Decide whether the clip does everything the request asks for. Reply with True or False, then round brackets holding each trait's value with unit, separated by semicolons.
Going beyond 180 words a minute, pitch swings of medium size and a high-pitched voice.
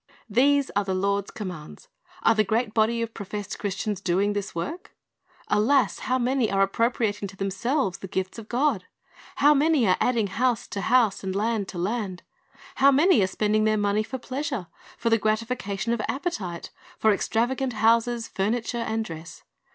True (200 wpm; 3.6 semitones; 220 Hz)